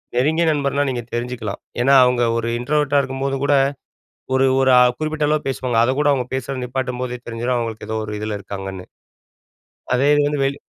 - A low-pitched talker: Yes, low, 130 Hz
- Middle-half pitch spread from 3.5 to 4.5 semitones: No, average, 2.9 semitones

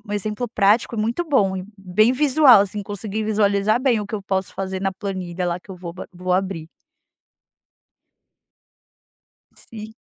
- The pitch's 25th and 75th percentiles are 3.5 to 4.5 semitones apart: No, narrow, 2.5 semitones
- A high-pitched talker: Yes, high, 200 Hz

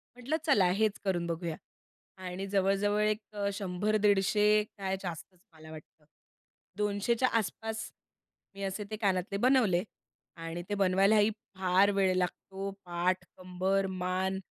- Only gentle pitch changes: Yes, narrow, 2.3 semitones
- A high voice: Yes, high, 195 Hz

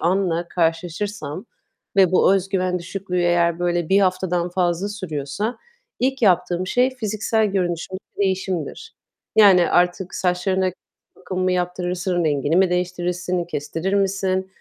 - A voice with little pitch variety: Yes, narrow, 1.8 semitones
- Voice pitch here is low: No, medium, 180 Hz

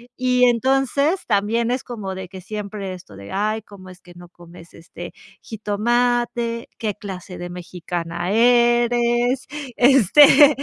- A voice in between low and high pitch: No, high, 215 Hz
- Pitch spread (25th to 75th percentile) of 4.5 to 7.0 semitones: Yes, average, 4.8 semitones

